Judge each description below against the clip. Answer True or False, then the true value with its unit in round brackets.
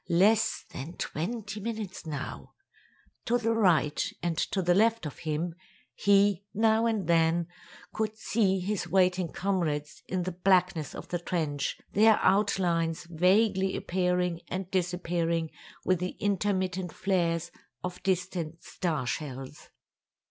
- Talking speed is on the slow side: True (125 wpm)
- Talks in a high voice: False (180 Hz)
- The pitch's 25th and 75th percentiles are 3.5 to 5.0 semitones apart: False (3.0 semitones)